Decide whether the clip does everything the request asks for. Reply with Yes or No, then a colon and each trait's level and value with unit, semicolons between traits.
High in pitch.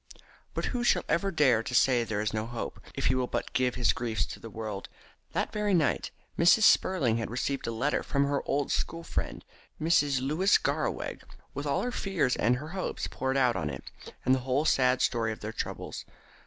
No: low, 130 Hz